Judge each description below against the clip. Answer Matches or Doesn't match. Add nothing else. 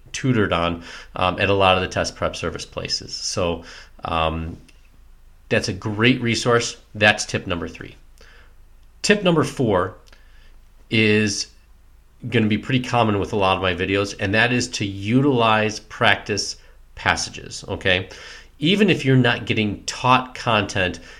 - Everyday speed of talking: Matches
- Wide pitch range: Matches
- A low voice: Matches